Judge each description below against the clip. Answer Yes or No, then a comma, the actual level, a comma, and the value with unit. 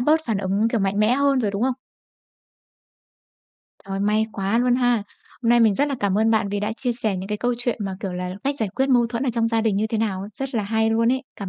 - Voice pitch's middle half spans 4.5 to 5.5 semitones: No, average, 3.2 semitones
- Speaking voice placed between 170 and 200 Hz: No, high, 225 Hz